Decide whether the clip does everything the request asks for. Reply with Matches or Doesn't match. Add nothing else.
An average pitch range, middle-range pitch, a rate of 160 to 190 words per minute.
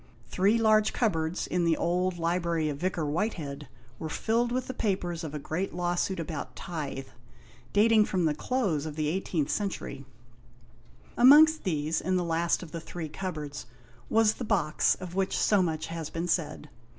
Matches